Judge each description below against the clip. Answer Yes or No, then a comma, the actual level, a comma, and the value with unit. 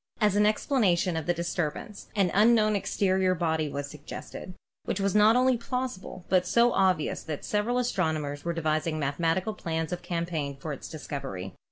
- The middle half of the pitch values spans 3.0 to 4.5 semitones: No, average, 4.9 semitones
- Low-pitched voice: No, medium, 180 Hz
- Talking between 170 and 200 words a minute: Yes, average, 175 wpm